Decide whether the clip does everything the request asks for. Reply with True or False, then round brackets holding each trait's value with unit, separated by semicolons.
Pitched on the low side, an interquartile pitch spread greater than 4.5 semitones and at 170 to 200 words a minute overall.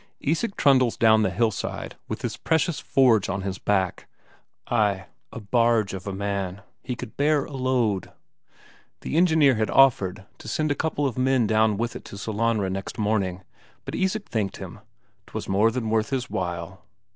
True (110 Hz; 5.0 semitones; 175 wpm)